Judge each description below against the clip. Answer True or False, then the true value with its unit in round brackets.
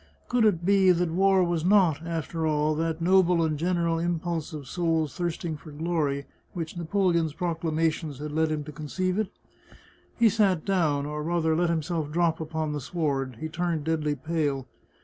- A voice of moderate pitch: True (165 Hz)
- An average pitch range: False (2.3 semitones)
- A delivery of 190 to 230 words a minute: False (175 wpm)